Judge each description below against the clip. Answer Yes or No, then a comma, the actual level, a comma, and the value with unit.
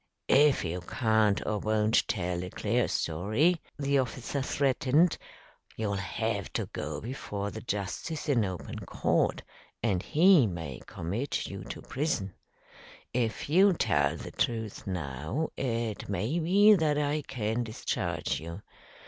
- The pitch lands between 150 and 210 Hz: No, low, 110 Hz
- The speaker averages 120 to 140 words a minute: Yes, slow, 135 wpm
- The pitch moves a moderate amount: No, wide, 6.7 semitones